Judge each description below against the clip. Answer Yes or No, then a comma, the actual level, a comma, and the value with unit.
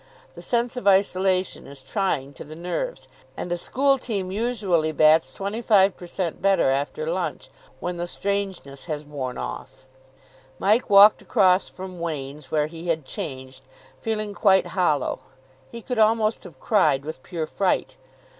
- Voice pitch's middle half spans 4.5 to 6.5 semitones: Yes, average, 5.0 semitones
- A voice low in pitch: No, medium, 180 Hz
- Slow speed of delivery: No, average, 155 wpm